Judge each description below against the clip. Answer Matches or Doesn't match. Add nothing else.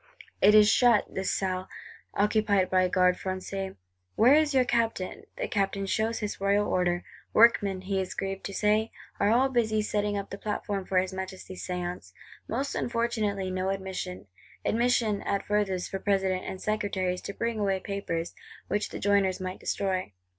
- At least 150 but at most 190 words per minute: Matches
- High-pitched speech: Matches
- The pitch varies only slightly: Matches